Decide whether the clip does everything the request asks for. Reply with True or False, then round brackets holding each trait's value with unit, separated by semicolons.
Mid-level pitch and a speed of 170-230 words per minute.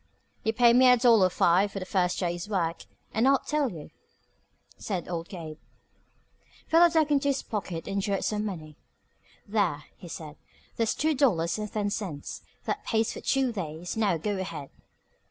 False (200 Hz; 175 wpm)